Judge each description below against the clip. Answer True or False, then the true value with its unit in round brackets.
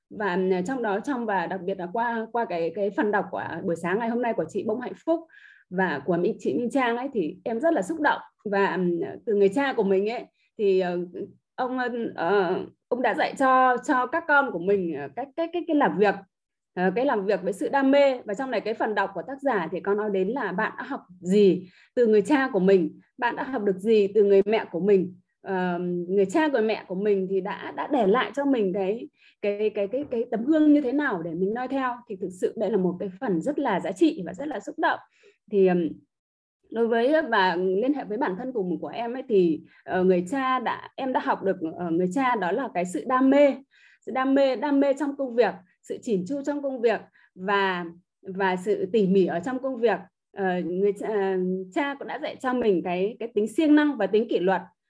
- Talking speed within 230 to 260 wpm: True (240 wpm)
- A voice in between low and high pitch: False (210 Hz)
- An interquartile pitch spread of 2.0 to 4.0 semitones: False (5.6 semitones)